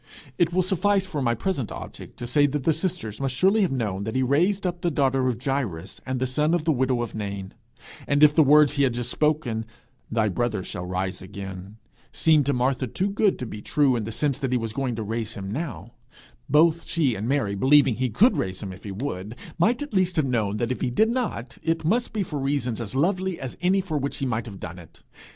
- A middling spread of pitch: No, wide, 6.4 semitones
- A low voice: Yes, low, 130 Hz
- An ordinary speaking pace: No, fast, 240 wpm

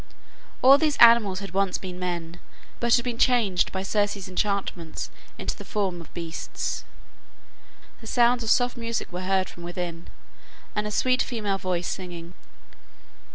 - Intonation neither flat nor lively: Yes, average, 4.5 semitones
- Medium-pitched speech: No, high, 195 Hz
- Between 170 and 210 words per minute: No, average, 155 wpm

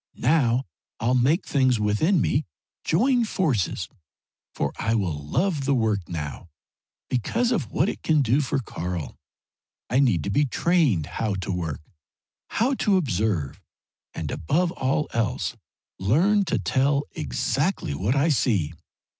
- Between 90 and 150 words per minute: Yes, average, 140 wpm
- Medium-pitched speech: No, low, 125 Hz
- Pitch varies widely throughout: Yes, wide, 8.2 semitones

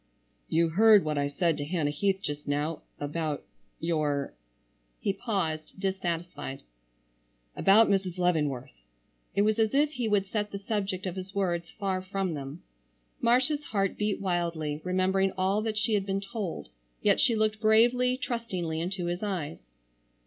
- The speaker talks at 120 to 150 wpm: Yes, average, 145 wpm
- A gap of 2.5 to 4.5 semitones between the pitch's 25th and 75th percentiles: No, average, 5.3 semitones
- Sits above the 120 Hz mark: Yes, medium, 185 Hz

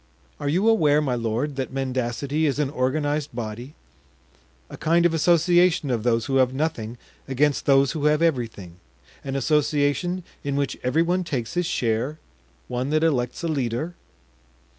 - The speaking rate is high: No, average, 160 wpm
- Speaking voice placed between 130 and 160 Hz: Yes, medium, 140 Hz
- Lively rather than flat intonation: No, average, 4.0 semitones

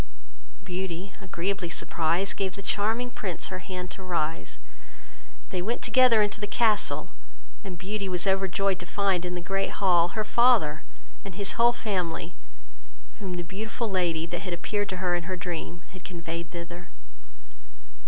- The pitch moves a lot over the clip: No, narrow, 2.6 semitones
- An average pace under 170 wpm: Yes, average, 155 wpm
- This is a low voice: No, medium, 185 Hz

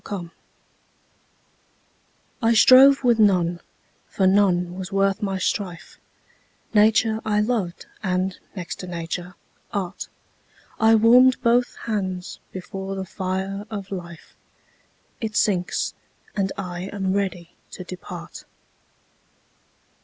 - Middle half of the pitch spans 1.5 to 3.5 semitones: Yes, average, 2.8 semitones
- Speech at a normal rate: No, slow, 110 wpm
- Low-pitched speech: No, high, 195 Hz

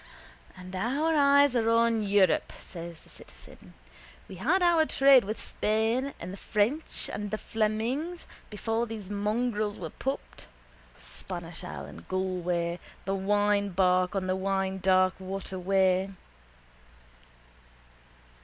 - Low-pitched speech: No, high, 205 Hz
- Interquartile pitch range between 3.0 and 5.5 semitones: Yes, average, 3.8 semitones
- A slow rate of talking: Yes, slow, 120 wpm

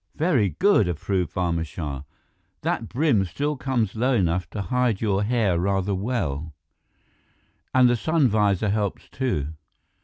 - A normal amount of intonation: No, wide, 5.7 semitones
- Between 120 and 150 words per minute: Yes, average, 140 wpm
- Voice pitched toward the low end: Yes, low, 105 Hz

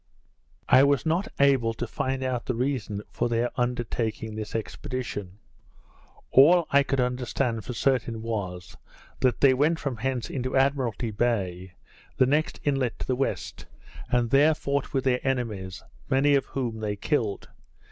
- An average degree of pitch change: Yes, average, 3.3 semitones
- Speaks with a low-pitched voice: Yes, low, 125 Hz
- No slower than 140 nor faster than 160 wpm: Yes, average, 155 wpm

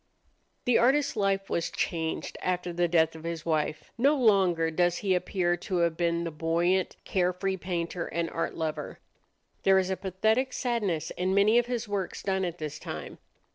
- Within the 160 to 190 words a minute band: Yes, average, 175 wpm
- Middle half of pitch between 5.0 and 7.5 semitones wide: No, average, 2.8 semitones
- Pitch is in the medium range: Yes, medium, 180 Hz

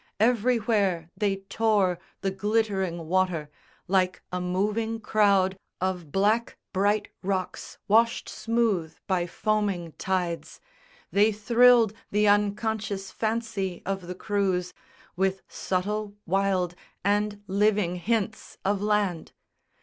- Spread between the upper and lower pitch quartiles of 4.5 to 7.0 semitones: No, narrow, 2.5 semitones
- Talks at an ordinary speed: No, slow, 105 wpm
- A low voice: No, high, 200 Hz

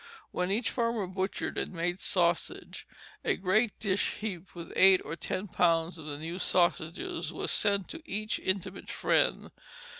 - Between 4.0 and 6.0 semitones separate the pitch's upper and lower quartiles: No, average, 3.3 semitones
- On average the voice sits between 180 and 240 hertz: Yes, medium, 185 Hz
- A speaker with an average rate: Yes, average, 155 wpm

